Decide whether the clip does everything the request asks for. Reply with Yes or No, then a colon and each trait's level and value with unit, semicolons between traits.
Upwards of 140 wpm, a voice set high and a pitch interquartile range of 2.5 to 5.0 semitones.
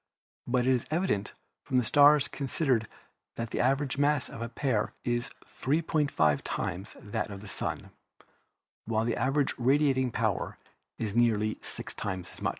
No: average, 155 wpm; low, 120 Hz; average, 4.3 semitones